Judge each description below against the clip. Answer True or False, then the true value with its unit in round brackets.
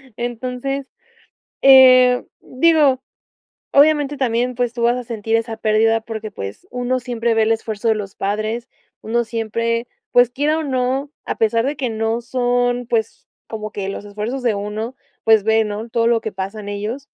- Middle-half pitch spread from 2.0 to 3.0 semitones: True (2.4 semitones)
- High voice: True (230 Hz)